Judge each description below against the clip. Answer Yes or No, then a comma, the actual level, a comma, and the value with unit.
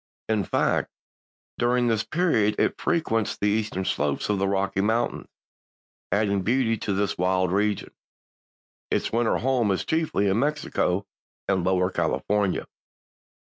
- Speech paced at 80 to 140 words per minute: Yes, slow, 135 wpm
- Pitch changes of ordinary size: Yes, average, 3.3 semitones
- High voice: No, low, 105 Hz